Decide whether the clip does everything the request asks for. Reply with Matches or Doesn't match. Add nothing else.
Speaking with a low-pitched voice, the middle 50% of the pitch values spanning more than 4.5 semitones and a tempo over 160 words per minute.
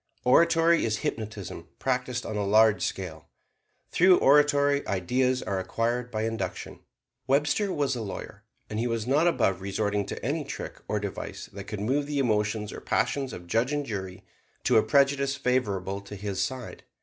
Matches